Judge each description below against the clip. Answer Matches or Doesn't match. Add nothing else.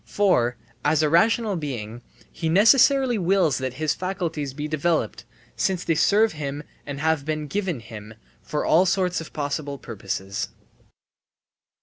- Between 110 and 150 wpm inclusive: Matches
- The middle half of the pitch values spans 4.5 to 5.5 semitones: Matches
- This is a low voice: Doesn't match